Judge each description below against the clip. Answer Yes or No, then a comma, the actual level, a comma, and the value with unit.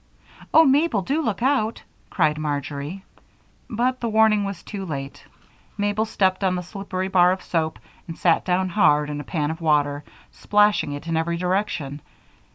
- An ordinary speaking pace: Yes, average, 165 wpm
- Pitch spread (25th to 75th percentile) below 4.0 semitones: No, average, 5.2 semitones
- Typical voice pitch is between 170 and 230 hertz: Yes, medium, 185 Hz